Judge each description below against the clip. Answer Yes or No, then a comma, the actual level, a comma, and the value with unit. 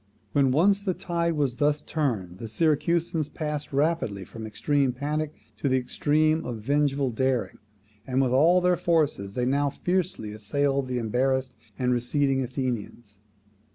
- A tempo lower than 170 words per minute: Yes, average, 155 wpm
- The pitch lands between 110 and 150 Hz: Yes, medium, 140 Hz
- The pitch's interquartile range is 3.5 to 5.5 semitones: Yes, average, 3.9 semitones